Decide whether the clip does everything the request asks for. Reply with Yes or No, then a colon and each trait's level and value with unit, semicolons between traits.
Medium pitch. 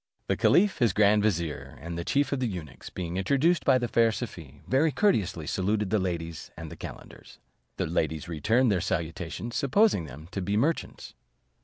No: low, 100 Hz